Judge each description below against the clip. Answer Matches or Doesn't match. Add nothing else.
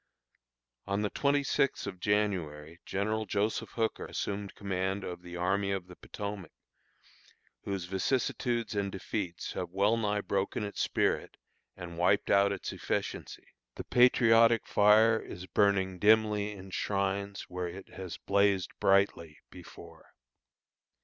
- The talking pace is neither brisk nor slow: Doesn't match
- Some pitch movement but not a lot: Doesn't match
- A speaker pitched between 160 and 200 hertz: Doesn't match